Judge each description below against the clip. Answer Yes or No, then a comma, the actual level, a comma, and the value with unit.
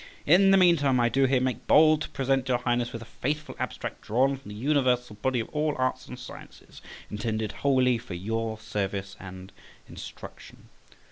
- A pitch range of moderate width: Yes, average, 3.7 semitones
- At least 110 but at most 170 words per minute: No, average, 180 wpm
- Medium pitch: No, low, 125 Hz